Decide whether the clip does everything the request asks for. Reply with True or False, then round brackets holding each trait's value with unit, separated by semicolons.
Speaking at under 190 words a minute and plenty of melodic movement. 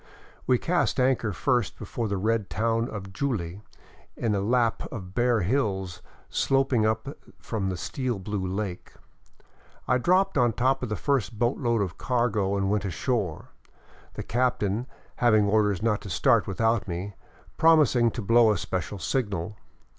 False (155 wpm; 3.9 semitones)